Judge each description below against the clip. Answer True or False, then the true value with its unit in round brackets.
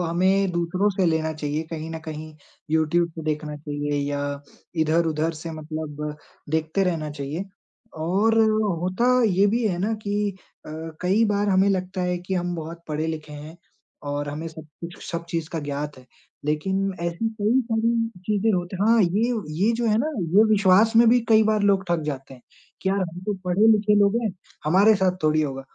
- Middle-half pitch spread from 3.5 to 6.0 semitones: True (4.6 semitones)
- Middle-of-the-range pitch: True (175 Hz)